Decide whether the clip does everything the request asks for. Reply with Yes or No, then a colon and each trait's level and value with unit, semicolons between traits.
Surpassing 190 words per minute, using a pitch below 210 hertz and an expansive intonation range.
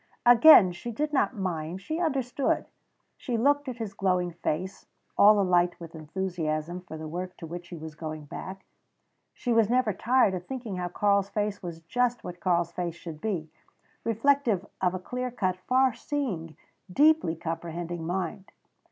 No: average, 165 wpm; medium, 185 Hz; wide, 5.7 semitones